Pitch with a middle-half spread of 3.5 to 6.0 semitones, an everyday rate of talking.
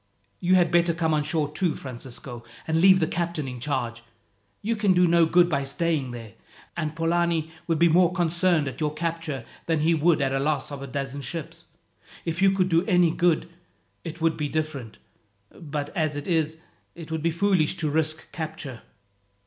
No: average, 2.7 semitones; average, 190 wpm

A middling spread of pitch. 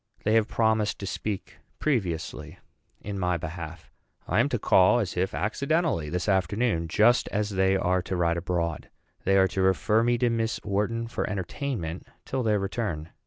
Yes: average, 4.2 semitones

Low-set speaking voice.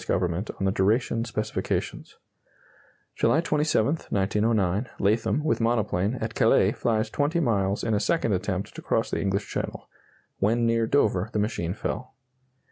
Yes: low, 110 Hz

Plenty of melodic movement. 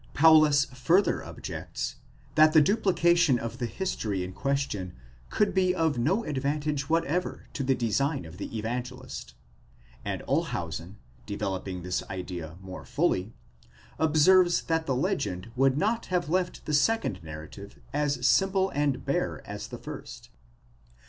Yes: wide, 7.5 semitones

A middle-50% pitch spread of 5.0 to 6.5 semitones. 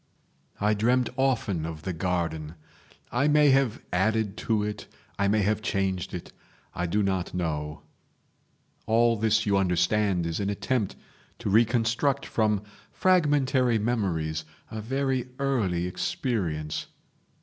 Yes: average, 5.3 semitones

